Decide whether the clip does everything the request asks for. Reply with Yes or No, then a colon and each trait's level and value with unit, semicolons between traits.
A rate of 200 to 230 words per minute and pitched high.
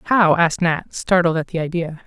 No: fast, 205 wpm; medium, 170 Hz